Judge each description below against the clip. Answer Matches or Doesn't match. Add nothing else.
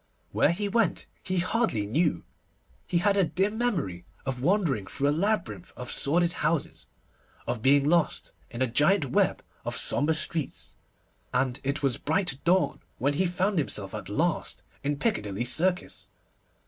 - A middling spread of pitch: Doesn't match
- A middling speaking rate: Matches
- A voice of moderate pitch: Matches